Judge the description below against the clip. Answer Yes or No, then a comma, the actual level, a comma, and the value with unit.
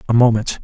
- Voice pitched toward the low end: Yes, low, 115 Hz